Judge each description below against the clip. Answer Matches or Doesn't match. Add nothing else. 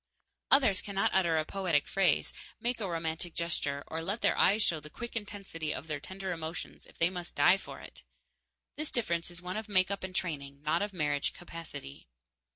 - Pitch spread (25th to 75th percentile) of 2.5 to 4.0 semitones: Matches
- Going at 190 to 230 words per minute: Matches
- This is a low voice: Doesn't match